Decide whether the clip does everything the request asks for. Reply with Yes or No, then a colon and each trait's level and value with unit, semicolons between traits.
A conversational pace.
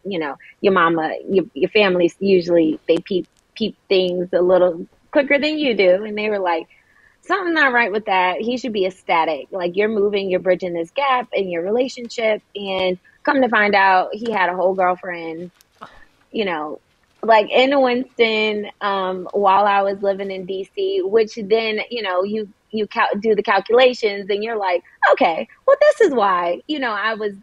Yes: average, 185 wpm